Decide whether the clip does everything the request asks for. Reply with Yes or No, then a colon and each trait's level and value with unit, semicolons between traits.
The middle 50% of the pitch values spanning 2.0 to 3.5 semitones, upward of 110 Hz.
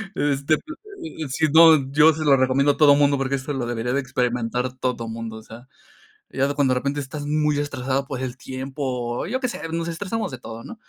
Yes: average, 2.9 semitones; medium, 140 Hz